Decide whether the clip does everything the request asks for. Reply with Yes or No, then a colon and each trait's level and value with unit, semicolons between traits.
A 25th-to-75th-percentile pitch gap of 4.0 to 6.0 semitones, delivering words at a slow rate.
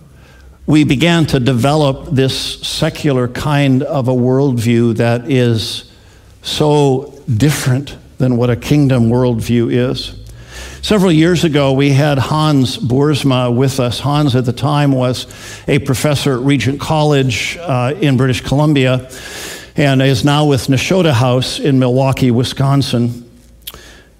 No: average, 2.8 semitones; slow, 130 wpm